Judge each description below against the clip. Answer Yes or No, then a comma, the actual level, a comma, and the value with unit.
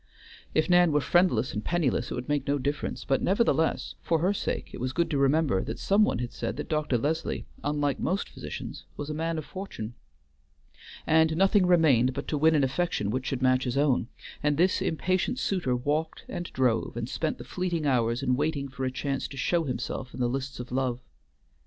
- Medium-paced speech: No, fast, 210 wpm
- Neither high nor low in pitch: Yes, medium, 145 Hz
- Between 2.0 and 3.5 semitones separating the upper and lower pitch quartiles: No, average, 4.3 semitones